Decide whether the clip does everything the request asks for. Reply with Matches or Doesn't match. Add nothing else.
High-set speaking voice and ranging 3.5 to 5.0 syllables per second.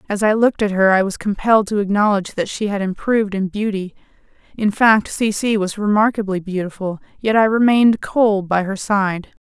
Doesn't match